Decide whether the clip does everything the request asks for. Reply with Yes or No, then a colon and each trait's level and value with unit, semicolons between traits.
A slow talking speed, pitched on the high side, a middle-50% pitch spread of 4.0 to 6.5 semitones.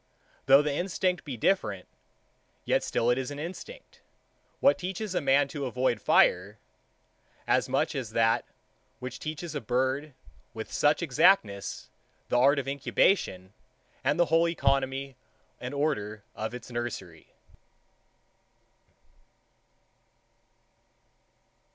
No: slow, 120 wpm; low, 135 Hz; average, 4.5 semitones